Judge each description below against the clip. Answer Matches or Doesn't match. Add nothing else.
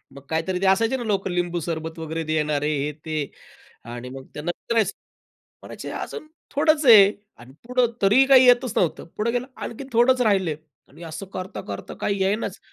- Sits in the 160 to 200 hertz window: Matches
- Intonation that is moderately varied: Doesn't match